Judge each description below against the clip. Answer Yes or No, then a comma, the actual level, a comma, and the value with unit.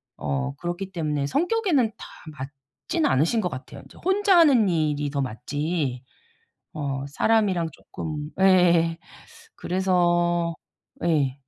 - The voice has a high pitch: No, medium, 170 Hz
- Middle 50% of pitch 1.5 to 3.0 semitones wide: No, average, 5.2 semitones